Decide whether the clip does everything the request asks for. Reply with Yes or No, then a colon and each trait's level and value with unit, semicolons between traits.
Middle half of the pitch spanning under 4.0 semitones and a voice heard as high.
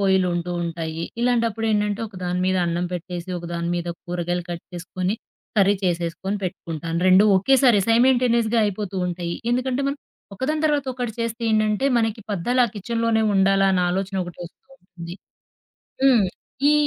No: average, 4.7 semitones; high, 195 Hz